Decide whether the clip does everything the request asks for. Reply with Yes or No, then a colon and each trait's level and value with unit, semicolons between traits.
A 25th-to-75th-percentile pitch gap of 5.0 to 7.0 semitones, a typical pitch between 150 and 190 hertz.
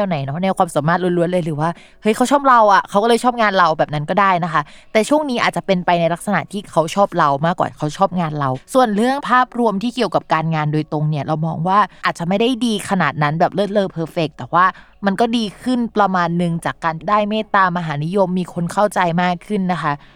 No: average, 4.3 semitones; medium, 185 Hz